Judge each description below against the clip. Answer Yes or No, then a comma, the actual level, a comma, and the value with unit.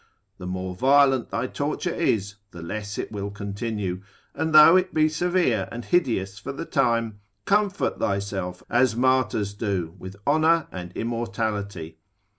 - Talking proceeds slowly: No, average, 145 wpm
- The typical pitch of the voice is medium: No, low, 110 Hz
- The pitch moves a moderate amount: No, wide, 5.8 semitones